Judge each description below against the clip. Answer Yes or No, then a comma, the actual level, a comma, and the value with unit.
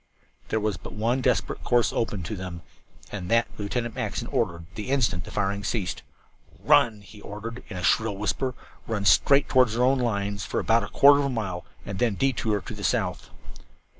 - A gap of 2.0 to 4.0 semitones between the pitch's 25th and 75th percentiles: Yes, average, 3.4 semitones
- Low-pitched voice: Yes, low, 110 Hz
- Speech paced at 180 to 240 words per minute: Yes, average, 195 wpm